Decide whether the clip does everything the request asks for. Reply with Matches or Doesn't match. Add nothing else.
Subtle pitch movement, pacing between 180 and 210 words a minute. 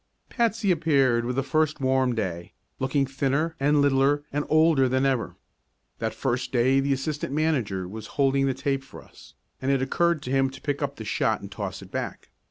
Matches